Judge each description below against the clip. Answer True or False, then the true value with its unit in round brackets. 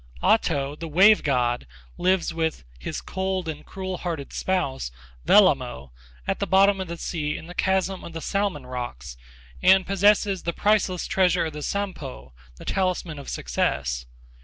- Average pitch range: False (5.7 semitones)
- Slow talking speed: False (160 wpm)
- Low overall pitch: False (170 Hz)